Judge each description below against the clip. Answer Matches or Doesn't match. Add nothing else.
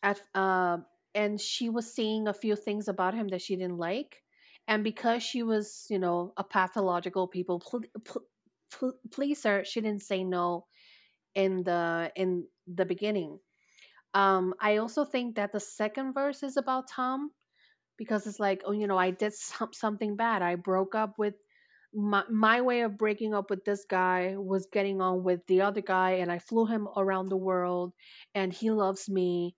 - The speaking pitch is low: Doesn't match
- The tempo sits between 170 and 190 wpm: Matches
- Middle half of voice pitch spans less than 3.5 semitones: Matches